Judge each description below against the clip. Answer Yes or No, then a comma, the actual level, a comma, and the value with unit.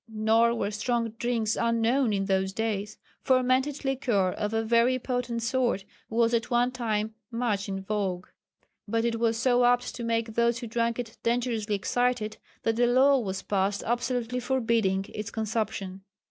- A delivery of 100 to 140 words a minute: No, average, 160 wpm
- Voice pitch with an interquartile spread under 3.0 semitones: Yes, narrow, 2.4 semitones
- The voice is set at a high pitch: Yes, high, 230 Hz